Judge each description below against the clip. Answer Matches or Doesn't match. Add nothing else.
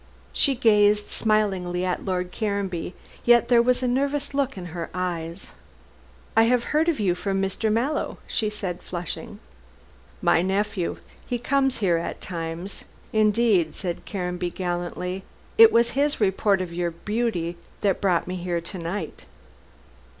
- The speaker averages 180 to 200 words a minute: Doesn't match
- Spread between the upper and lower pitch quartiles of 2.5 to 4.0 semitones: Doesn't match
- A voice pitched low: Doesn't match